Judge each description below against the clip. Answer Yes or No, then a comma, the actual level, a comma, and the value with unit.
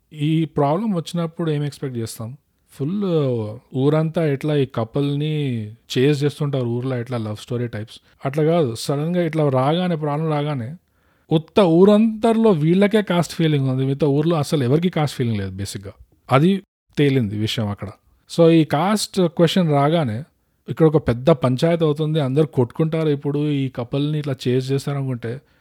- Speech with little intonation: No, average, 4.2 semitones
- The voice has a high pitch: No, medium, 145 Hz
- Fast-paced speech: Yes, fast, 145 wpm